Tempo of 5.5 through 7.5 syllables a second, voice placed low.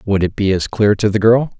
Yes: 5.6 syllables/s; low, 105 Hz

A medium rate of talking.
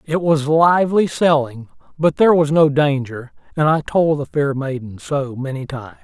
Yes: average, 180 wpm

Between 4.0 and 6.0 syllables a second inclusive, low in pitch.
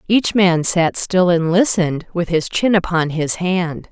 No: 4.1 syllables/s; medium, 175 Hz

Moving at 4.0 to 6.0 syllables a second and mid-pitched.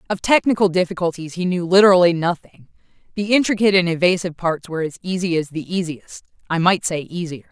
No: 6.3 syllables/s; medium, 175 Hz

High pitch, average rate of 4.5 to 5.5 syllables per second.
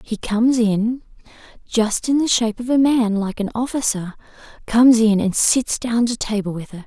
Yes: high, 230 Hz; 5.0 syllables/s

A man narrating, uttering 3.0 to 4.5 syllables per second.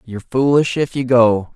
No: male; 4.8 syllables/s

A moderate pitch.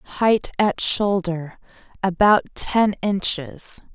No: high, 195 Hz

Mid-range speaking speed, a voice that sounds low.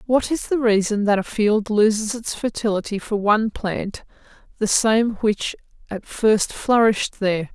No: average, 160 wpm; high, 215 Hz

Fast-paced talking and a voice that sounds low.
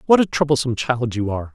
Yes: fast, 235 wpm; low, 130 Hz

